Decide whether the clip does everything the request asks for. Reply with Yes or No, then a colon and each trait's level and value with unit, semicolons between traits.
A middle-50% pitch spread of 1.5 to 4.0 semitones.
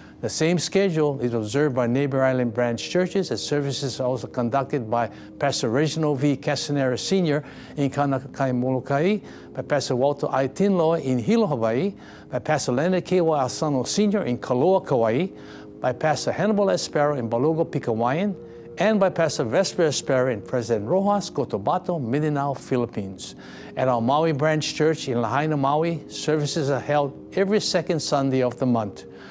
No: average, 4.6 semitones